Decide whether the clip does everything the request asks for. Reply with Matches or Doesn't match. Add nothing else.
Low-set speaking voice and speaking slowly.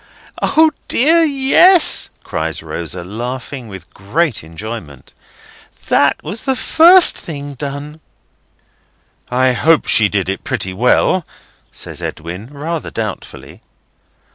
Matches